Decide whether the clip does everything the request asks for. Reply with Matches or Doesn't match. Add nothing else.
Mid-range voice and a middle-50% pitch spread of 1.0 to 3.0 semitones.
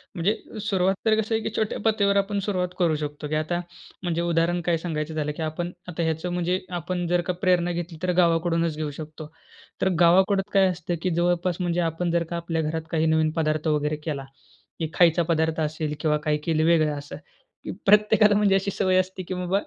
Matches